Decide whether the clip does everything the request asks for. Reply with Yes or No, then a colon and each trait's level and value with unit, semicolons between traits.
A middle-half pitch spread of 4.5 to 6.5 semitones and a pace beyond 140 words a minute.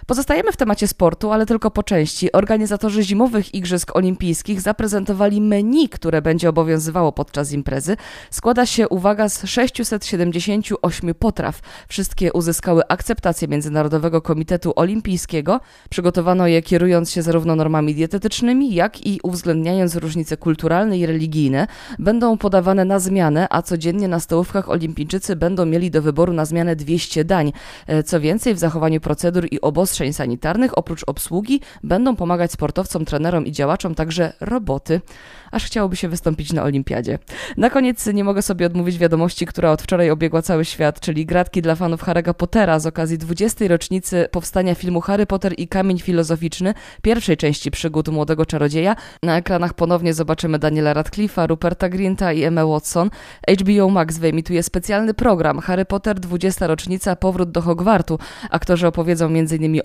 No: average, 3.5 semitones; average, 150 wpm